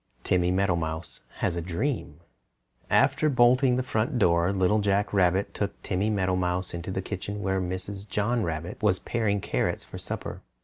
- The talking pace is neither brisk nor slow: Yes, average, 160 wpm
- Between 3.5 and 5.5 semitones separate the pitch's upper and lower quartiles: No, average, 2.9 semitones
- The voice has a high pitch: No, very low, 95 Hz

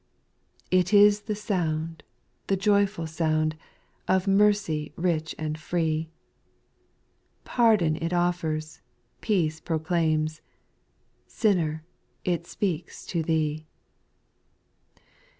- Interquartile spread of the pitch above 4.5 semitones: No, average, 3.7 semitones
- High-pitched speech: No, medium, 165 Hz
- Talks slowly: Yes, slow, 95 wpm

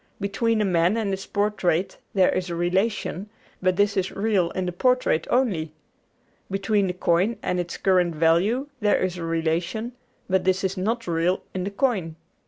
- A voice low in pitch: No, high, 190 Hz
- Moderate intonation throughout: Yes, average, 3.0 semitones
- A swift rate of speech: No, average, 180 wpm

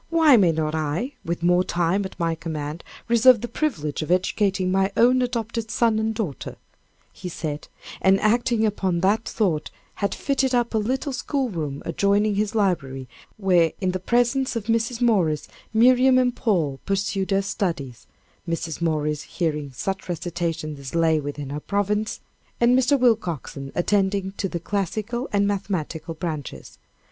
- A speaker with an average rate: Yes, average, 155 wpm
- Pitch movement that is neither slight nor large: No, wide, 5.7 semitones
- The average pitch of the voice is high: Yes, high, 195 Hz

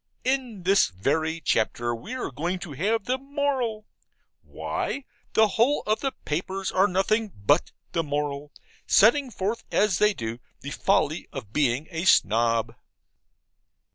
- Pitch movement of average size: No, wide, 7.6 semitones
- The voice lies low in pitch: No, medium, 185 Hz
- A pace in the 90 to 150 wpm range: Yes, average, 140 wpm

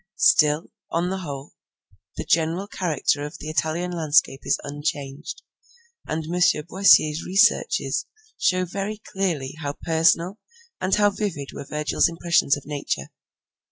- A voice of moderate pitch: Yes, medium, 165 Hz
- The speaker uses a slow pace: Yes, slow, 130 wpm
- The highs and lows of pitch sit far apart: No, average, 3.7 semitones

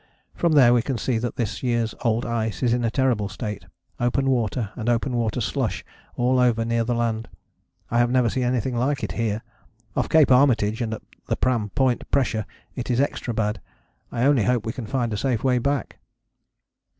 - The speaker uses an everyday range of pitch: No, narrow, 2.3 semitones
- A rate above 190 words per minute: Yes, average, 200 wpm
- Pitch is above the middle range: No, low, 120 Hz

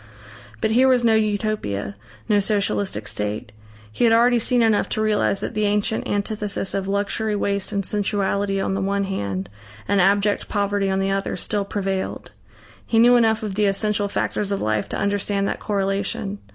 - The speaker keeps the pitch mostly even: Yes, narrow, 1.6 semitones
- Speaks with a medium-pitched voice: No, high, 200 Hz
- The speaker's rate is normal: Yes, average, 180 wpm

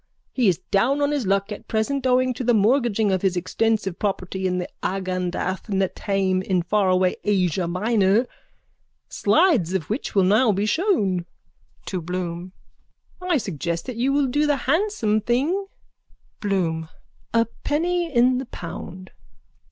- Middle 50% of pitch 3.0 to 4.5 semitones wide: No, wide, 5.5 semitones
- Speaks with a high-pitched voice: Yes, high, 205 Hz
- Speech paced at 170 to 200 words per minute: No, average, 145 wpm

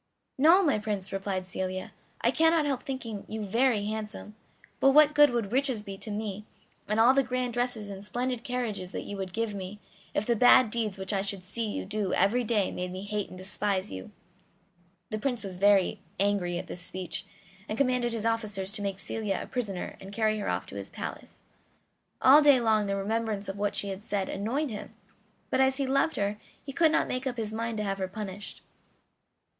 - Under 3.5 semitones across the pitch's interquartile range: No, average, 3.9 semitones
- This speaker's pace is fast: Yes, fast, 210 wpm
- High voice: Yes, high, 215 Hz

